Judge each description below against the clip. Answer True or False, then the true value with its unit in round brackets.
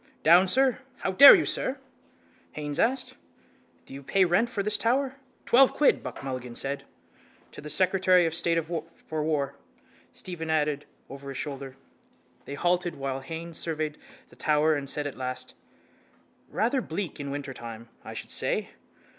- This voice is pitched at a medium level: True (160 Hz)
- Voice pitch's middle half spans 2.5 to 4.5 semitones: False (4.9 semitones)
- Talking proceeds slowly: False (155 wpm)